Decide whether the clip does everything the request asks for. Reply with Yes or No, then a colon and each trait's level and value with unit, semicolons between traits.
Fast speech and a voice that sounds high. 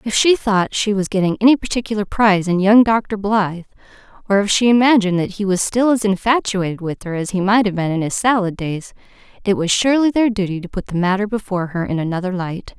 Yes: fast, 225 wpm; high, 200 Hz